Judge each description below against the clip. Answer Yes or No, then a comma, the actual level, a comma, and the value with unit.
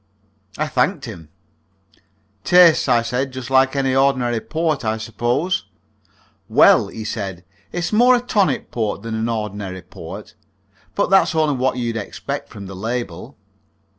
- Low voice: Yes, low, 125 Hz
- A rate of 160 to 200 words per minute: No, average, 145 wpm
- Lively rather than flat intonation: Yes, wide, 5.7 semitones